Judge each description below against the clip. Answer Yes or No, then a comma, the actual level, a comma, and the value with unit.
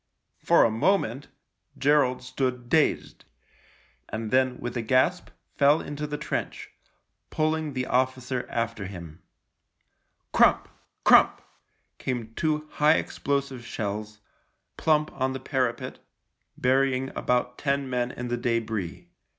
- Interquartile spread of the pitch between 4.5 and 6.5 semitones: No, average, 3.2 semitones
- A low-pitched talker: Yes, low, 130 Hz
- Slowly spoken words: Yes, slow, 125 wpm